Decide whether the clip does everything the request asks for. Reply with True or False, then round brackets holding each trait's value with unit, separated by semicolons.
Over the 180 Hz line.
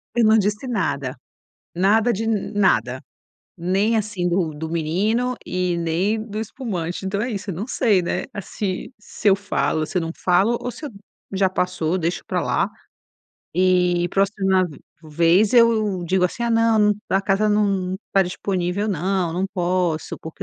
True (190 Hz)